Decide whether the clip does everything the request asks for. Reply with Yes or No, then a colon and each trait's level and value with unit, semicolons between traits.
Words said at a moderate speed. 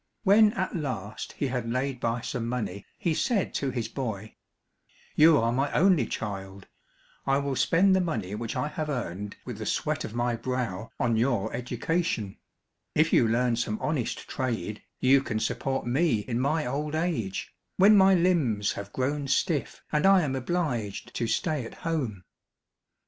Yes: average, 170 wpm